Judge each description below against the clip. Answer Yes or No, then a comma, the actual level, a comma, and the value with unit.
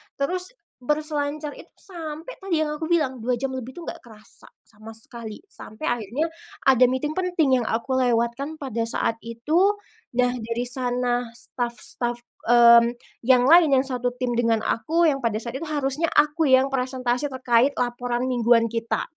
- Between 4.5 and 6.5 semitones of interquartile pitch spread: No, average, 4.0 semitones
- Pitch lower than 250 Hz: No, very high, 255 Hz